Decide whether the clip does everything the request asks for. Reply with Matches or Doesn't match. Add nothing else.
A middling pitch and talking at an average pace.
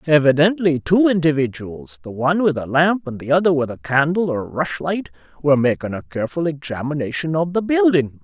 Matches